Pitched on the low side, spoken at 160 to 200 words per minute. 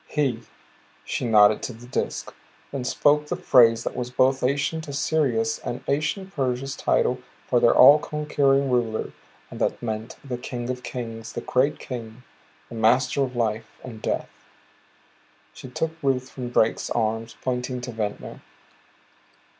No: low, 125 Hz; average, 145 wpm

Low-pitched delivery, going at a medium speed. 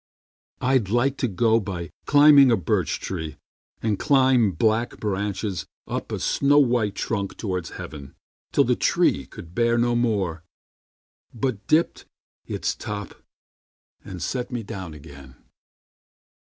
No: low, 110 Hz; slow, 130 wpm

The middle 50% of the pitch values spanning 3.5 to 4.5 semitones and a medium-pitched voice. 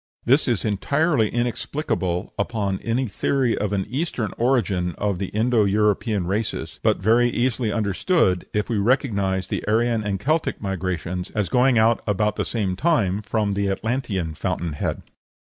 No: average, 3.9 semitones; low, 105 Hz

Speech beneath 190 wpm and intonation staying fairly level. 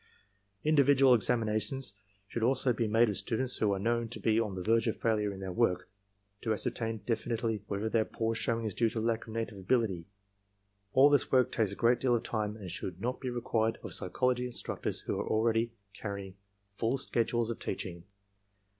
No: average, 195 wpm; narrow, 2.3 semitones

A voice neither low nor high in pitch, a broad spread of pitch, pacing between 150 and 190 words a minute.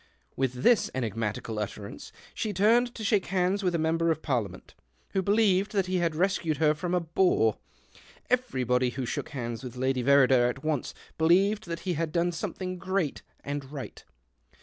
Yes: medium, 160 Hz; wide, 6.3 semitones; average, 170 wpm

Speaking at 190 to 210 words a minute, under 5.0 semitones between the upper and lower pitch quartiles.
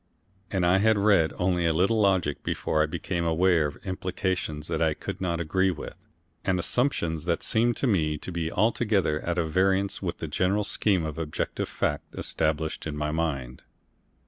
No: average, 175 wpm; average, 3.4 semitones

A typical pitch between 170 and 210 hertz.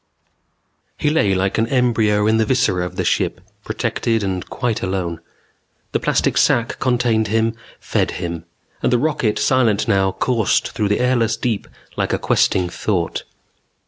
No: low, 110 Hz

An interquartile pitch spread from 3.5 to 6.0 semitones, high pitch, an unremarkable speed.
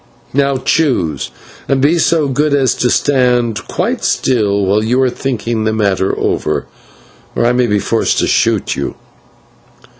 No: average, 4.2 semitones; low, 125 Hz; average, 155 wpm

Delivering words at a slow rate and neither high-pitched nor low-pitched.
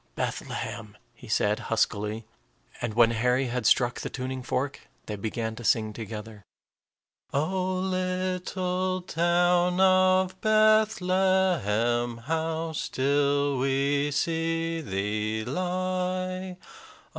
Yes: slow, 100 wpm; medium, 145 Hz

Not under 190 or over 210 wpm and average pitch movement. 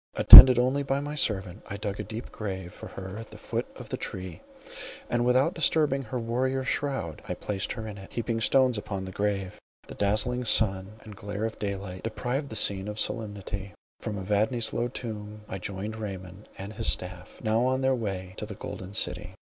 Yes: average, 195 wpm; average, 3.9 semitones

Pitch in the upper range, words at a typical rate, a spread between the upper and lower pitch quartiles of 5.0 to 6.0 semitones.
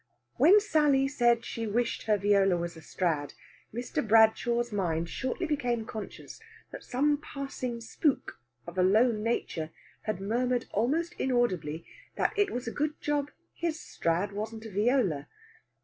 Yes: high, 230 Hz; average, 150 wpm; wide, 5.4 semitones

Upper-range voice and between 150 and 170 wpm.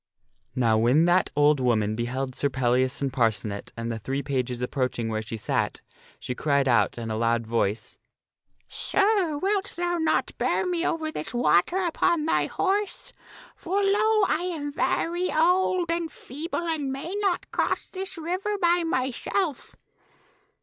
Yes: very high, 265 Hz; average, 155 wpm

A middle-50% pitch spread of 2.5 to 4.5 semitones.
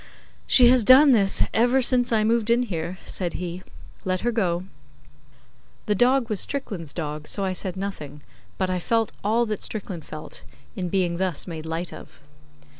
No: average, 5.2 semitones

